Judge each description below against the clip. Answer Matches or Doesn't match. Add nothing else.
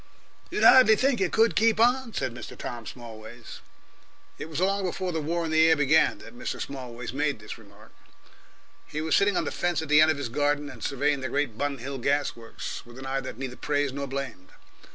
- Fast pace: Matches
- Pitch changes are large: Doesn't match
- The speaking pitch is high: Doesn't match